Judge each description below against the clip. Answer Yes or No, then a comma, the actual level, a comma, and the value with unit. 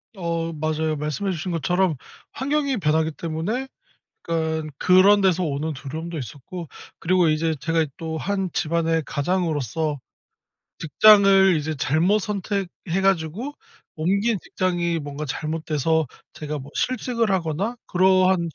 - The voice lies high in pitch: No, medium, 165 Hz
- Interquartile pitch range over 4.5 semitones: No, average, 3.5 semitones